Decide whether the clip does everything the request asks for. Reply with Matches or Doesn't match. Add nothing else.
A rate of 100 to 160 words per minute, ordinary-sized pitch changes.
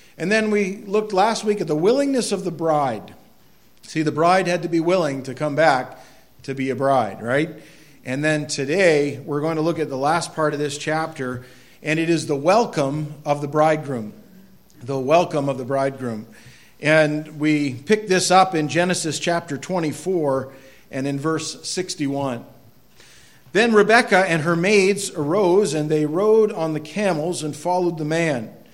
Doesn't match